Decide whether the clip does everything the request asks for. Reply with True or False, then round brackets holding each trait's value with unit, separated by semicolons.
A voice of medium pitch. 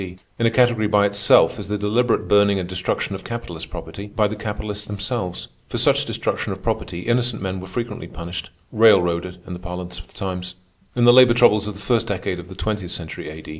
False (100 Hz)